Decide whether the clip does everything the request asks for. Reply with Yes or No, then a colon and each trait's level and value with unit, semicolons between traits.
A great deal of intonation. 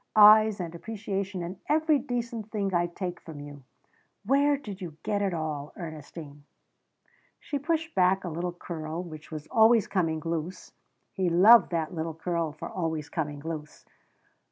No: average, 5.0 semitones